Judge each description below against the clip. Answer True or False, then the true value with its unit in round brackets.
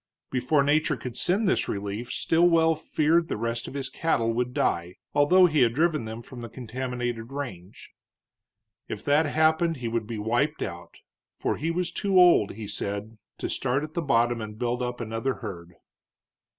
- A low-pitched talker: True (125 Hz)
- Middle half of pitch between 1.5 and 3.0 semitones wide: False (5.5 semitones)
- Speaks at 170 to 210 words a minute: True (175 wpm)